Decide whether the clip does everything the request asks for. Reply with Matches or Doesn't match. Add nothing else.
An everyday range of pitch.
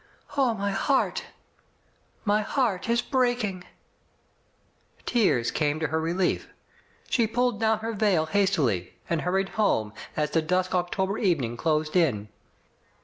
Doesn't match